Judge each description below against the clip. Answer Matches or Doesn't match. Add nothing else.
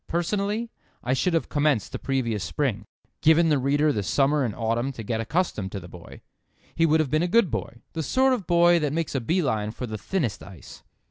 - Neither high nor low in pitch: Matches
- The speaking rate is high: Matches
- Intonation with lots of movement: Matches